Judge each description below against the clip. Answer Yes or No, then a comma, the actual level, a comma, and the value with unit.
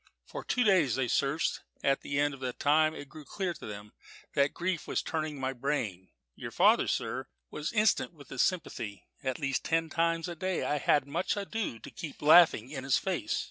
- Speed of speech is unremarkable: No, fast, 210 wpm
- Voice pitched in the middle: Yes, medium, 150 Hz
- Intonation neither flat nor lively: Yes, average, 4.0 semitones